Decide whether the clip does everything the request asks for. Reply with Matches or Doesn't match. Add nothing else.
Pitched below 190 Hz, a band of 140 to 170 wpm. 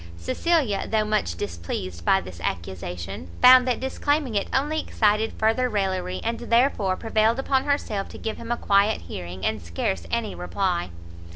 Doesn't match